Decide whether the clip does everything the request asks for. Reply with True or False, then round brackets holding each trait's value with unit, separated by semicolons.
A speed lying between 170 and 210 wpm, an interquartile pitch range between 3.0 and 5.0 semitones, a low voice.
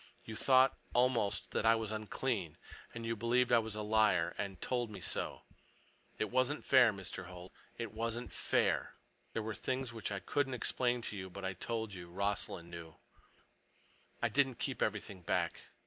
True (175 wpm; 3.7 semitones; 110 Hz)